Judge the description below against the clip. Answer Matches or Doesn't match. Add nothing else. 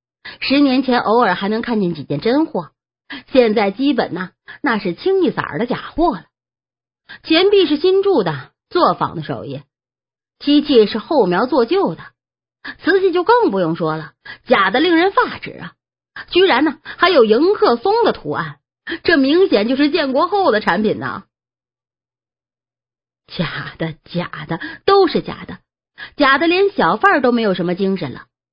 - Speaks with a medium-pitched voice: Doesn't match